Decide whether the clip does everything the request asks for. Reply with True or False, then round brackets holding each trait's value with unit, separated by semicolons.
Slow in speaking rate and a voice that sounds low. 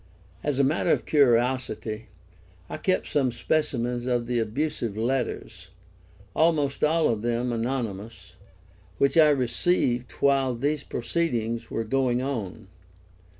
True (120 wpm; 125 Hz)